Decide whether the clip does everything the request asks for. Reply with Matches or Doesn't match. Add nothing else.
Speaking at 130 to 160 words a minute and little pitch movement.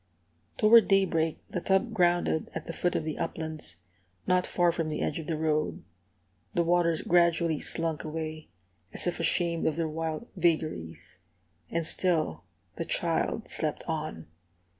Matches